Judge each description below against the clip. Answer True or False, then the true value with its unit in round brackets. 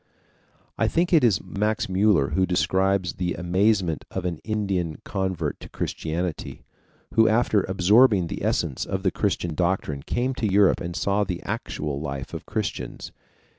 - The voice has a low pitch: True (95 Hz)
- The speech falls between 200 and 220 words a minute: False (155 wpm)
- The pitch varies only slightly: False (3.3 semitones)